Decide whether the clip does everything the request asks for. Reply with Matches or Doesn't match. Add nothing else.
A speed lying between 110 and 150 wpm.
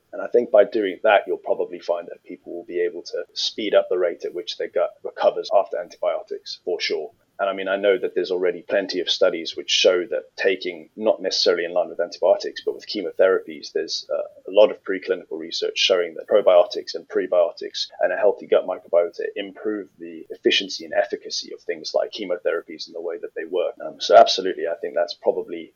Doesn't match